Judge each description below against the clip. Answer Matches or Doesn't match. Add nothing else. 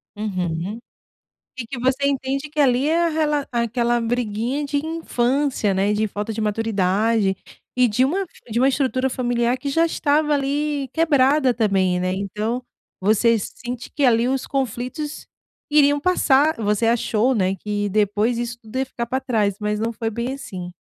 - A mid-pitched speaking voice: Doesn't match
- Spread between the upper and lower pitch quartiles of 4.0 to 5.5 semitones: Matches